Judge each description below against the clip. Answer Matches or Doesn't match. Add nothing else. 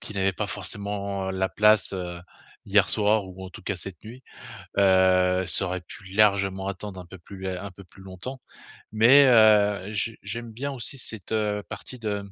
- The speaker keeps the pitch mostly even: Matches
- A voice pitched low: Matches